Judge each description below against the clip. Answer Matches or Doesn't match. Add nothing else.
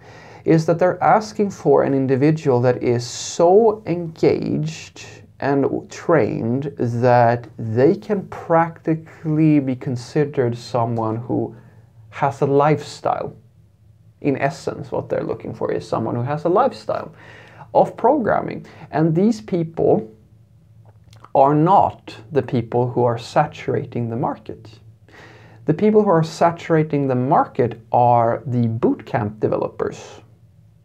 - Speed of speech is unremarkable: Doesn't match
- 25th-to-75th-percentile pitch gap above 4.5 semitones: Matches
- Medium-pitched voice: Doesn't match